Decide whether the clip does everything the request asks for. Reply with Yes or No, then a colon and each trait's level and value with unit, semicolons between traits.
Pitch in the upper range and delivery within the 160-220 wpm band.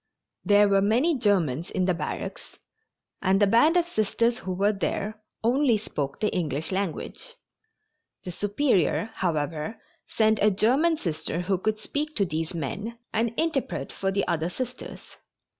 No: high, 205 Hz; average, 150 wpm